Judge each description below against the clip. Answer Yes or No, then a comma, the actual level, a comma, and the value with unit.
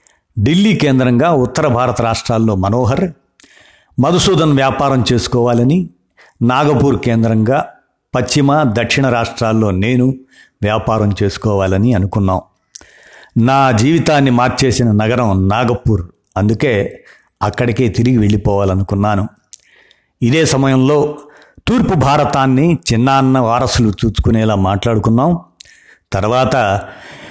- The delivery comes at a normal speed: Yes, average, 80 wpm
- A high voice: No, low, 120 Hz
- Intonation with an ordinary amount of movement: Yes, average, 3.8 semitones